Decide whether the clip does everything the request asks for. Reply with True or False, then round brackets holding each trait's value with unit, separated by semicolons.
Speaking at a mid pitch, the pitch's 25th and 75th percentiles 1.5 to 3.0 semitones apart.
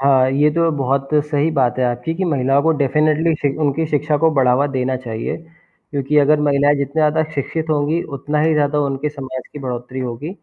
True (145 Hz; 2.4 semitones)